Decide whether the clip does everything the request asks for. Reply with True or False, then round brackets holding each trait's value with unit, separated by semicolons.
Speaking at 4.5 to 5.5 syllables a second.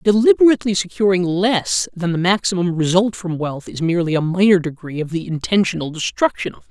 False (5.9 syllables/s)